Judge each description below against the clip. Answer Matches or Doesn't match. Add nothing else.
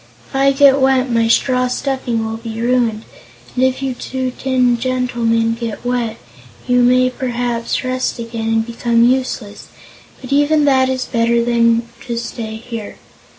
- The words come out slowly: Doesn't match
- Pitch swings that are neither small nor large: Doesn't match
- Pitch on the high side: Matches